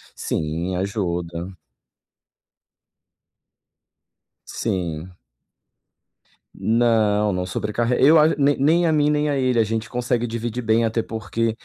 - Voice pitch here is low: Yes, low, 115 Hz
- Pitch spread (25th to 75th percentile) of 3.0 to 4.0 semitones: No, average, 4.8 semitones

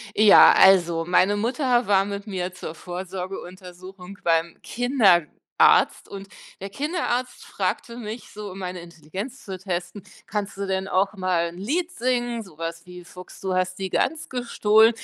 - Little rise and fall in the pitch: No, average, 3.5 semitones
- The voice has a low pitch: No, high, 195 Hz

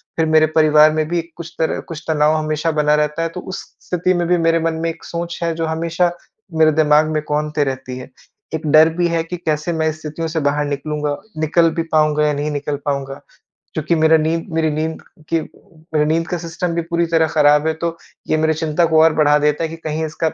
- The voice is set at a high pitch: No, medium, 160 Hz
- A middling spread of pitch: No, narrow, 1.5 semitones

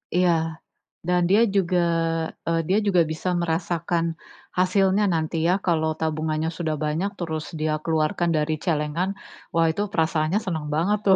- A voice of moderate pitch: Yes, medium, 165 Hz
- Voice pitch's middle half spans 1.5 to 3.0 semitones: Yes, narrow, 2.6 semitones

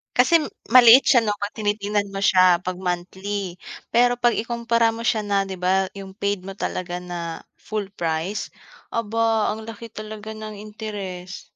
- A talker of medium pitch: No, high, 205 Hz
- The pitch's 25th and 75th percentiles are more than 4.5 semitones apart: No, average, 3.0 semitones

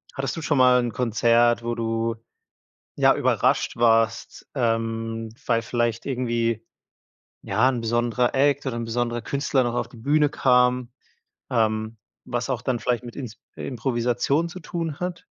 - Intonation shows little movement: Yes, narrow, 2.2 semitones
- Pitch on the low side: Yes, low, 120 Hz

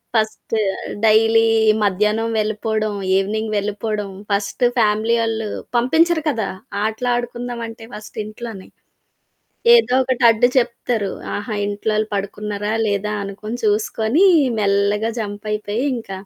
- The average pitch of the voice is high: Yes, high, 215 Hz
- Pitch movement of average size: No, narrow, 1.8 semitones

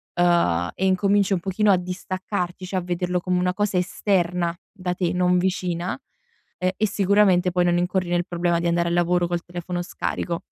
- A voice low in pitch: No, medium, 180 Hz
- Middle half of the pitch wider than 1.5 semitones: No, narrow, 1.2 semitones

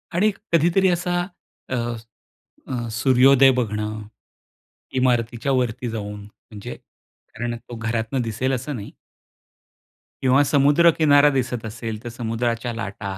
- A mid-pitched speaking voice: No, low, 120 Hz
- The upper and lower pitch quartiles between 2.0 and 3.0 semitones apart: No, average, 3.4 semitones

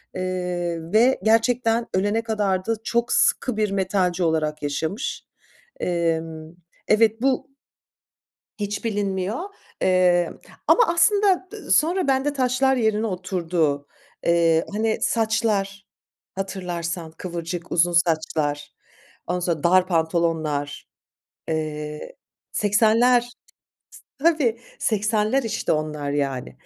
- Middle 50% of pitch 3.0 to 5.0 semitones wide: No, wide, 5.4 semitones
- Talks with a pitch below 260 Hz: Yes, medium, 185 Hz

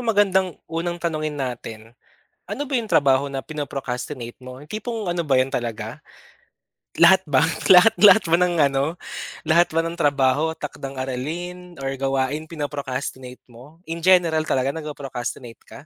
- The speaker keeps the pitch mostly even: No, average, 4.6 semitones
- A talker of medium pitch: Yes, medium, 150 Hz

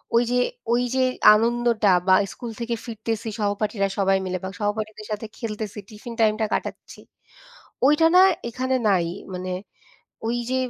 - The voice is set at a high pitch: Yes, high, 220 Hz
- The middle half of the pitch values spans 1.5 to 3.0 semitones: Yes, narrow, 2.5 semitones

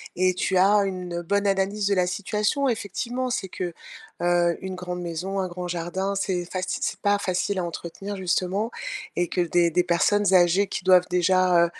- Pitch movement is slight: Yes, narrow, 2.2 semitones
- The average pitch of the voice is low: No, medium, 185 Hz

